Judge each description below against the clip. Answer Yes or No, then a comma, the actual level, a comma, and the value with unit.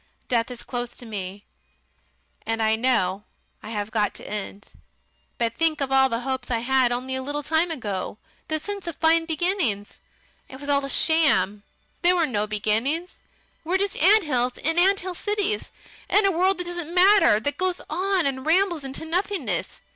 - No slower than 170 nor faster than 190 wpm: Yes, average, 180 wpm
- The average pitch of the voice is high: Yes, very high, 280 Hz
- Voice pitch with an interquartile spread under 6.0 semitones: No, wide, 7.4 semitones